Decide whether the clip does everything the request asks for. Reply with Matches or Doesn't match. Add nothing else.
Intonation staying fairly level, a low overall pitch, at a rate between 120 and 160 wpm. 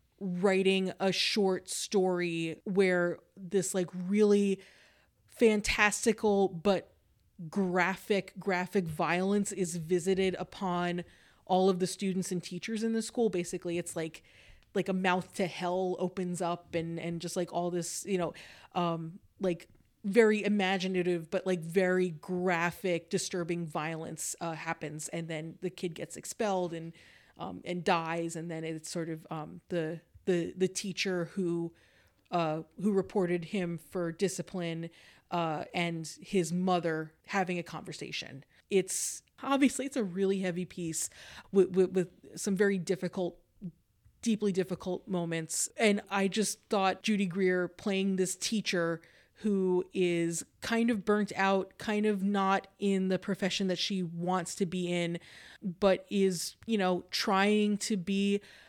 Doesn't match